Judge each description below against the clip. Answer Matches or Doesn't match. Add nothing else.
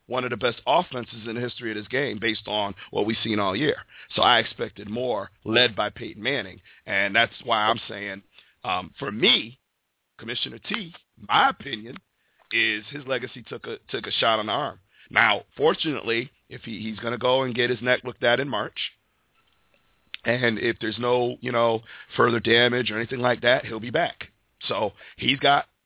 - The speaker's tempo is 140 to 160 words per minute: Doesn't match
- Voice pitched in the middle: Doesn't match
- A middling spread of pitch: Doesn't match